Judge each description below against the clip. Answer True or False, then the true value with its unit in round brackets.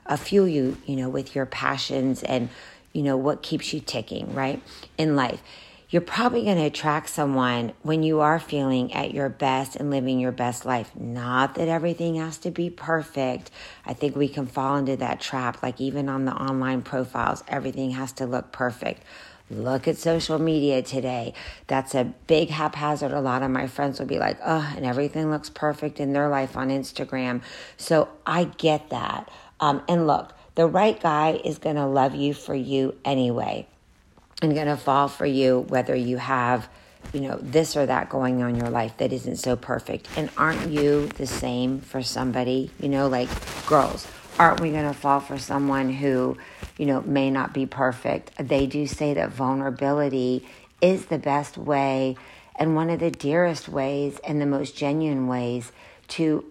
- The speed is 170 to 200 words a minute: True (185 wpm)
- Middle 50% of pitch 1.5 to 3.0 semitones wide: True (2.5 semitones)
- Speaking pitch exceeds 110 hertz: True (140 Hz)